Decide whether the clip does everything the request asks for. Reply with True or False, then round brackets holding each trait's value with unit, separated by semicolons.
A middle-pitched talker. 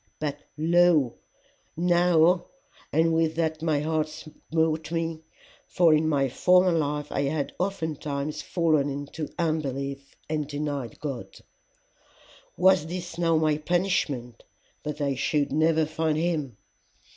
True (155 Hz)